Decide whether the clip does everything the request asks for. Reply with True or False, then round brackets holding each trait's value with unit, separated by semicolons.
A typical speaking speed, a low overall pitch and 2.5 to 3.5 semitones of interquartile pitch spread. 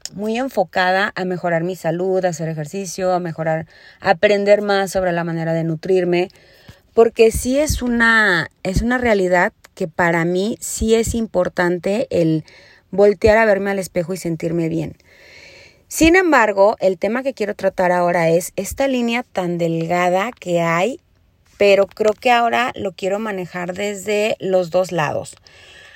False (155 wpm; 190 Hz; 3.1 semitones)